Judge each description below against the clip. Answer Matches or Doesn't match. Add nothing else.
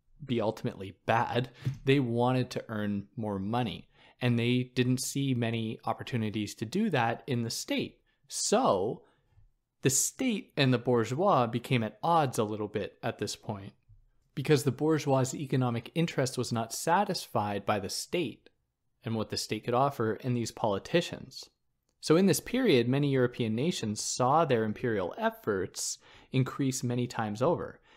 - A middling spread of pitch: Matches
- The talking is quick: Doesn't match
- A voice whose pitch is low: Matches